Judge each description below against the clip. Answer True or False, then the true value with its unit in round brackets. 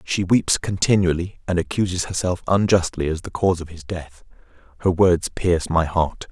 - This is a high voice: False (90 Hz)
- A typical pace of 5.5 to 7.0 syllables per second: False (5.1 syllables/s)